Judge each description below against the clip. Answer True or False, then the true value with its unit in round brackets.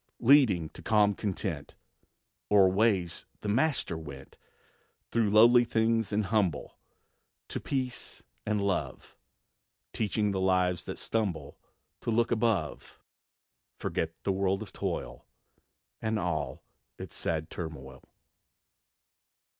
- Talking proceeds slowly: True (110 wpm)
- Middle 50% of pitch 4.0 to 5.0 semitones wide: True (4.4 semitones)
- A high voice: False (100 Hz)